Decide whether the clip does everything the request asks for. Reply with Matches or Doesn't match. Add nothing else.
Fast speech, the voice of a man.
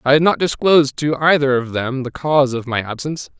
Matches